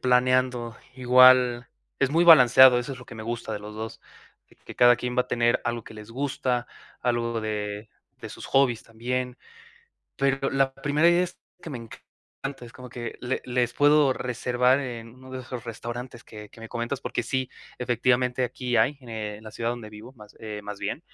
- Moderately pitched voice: No, low, 125 Hz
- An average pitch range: No, narrow, 1.8 semitones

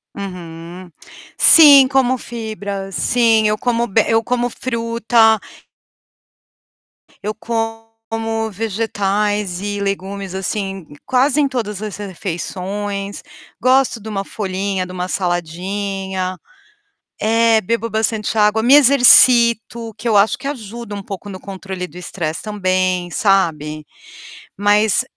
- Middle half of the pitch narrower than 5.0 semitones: Yes, average, 3.1 semitones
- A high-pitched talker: Yes, high, 210 Hz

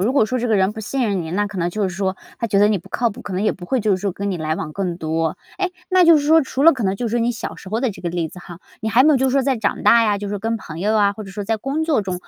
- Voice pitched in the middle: No, high, 210 Hz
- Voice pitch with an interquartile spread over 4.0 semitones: Yes, average, 4.5 semitones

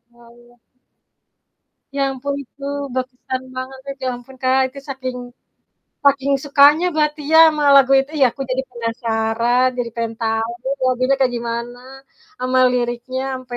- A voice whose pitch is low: No, very high, 255 Hz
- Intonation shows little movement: Yes, narrow, 2.1 semitones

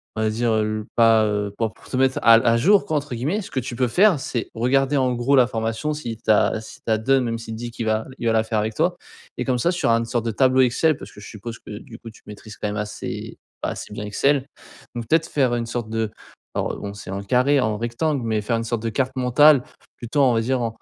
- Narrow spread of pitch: No, average, 3.0 semitones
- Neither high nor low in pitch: No, low, 115 Hz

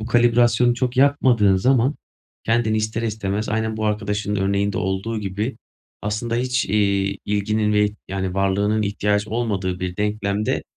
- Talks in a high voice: No, low, 105 Hz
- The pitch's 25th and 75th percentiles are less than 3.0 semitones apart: Yes, narrow, 2.4 semitones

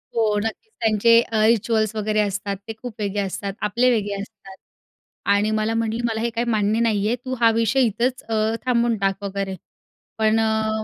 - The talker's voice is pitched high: Yes, high, 220 Hz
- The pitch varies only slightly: Yes, narrow, 2.0 semitones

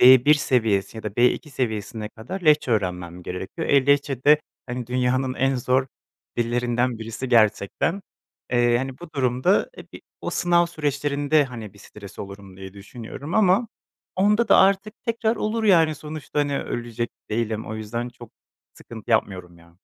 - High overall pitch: No, low, 125 Hz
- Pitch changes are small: No, wide, 5.5 semitones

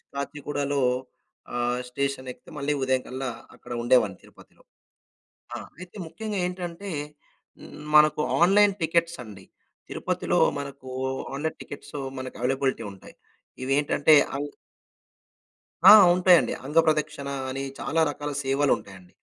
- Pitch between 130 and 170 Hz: Yes, medium, 140 Hz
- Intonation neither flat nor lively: Yes, average, 3.7 semitones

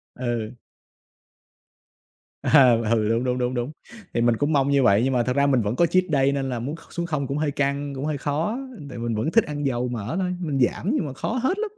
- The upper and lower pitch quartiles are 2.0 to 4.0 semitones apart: Yes, average, 3.7 semitones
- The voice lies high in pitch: No, low, 135 Hz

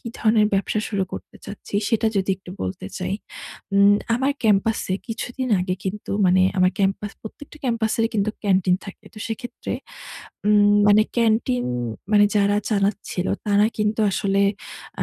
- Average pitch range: No, narrow, 2.1 semitones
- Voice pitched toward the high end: Yes, high, 205 Hz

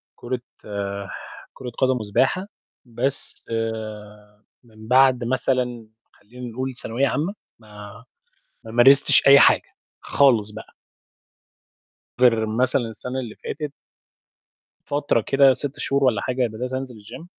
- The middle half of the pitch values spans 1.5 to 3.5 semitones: Yes, average, 2.9 semitones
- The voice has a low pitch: Yes, low, 125 Hz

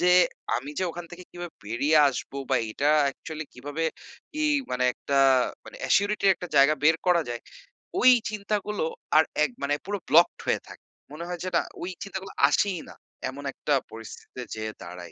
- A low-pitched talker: No, medium, 160 Hz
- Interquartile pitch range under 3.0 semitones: No, average, 4.9 semitones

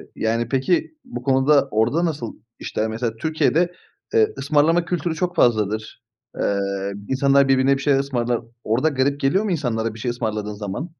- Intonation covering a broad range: Yes, wide, 5.9 semitones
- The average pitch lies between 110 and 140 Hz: Yes, low, 135 Hz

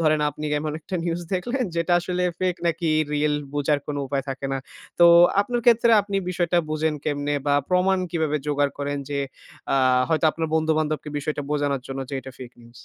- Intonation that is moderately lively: Yes, average, 3.4 semitones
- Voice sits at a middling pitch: Yes, medium, 155 Hz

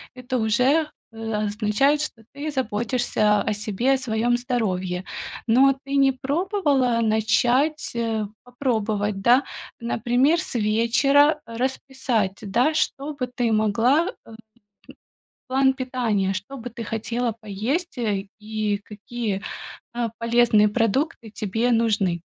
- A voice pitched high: Yes, high, 235 Hz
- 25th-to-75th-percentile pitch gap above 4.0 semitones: No, average, 3.7 semitones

